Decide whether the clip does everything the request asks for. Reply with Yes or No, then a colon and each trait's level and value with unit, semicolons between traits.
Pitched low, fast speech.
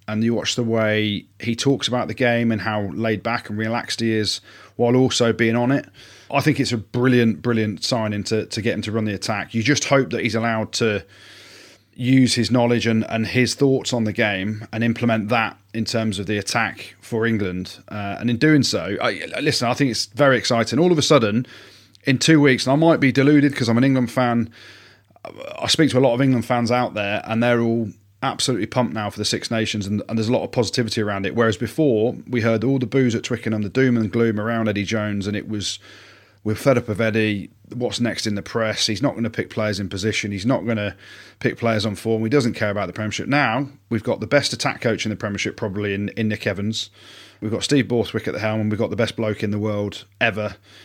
Yes: low, 115 Hz; fast, 245 wpm